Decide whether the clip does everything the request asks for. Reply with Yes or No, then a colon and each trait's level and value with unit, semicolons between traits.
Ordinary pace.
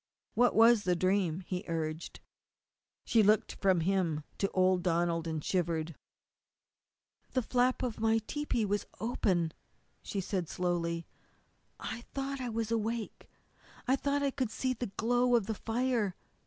Yes: average, 145 wpm